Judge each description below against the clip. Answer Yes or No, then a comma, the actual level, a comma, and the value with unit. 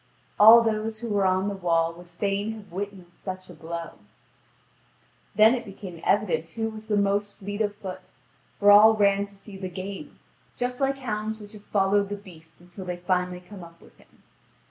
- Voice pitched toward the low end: No, high, 200 Hz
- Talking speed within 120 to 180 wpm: No, average, 190 wpm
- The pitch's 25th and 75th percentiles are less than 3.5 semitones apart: Yes, average, 2.8 semitones